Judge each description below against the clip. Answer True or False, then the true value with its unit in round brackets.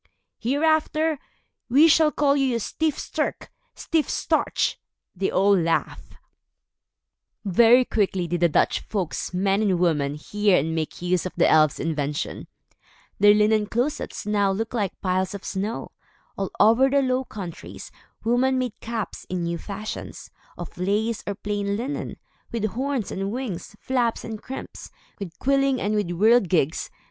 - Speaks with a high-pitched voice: True (210 Hz)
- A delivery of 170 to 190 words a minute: False (145 wpm)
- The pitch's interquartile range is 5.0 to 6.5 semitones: True (5.5 semitones)